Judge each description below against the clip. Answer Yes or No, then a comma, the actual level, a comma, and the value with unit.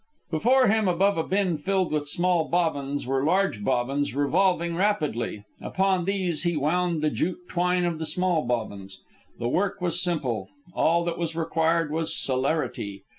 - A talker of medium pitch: Yes, medium, 165 Hz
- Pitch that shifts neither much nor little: Yes, average, 4.0 semitones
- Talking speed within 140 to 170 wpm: Yes, average, 160 wpm